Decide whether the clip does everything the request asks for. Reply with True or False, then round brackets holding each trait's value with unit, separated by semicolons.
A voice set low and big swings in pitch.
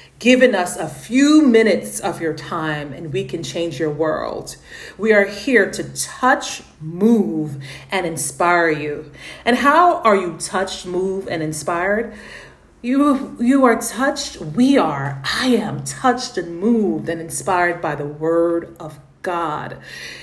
False (180 Hz; 6.8 semitones)